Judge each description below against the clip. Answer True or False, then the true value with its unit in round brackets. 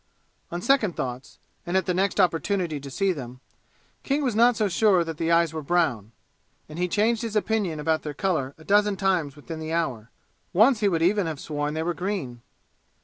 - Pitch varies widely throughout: False (4.9 semitones)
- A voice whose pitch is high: False (175 Hz)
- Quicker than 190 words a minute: True (205 wpm)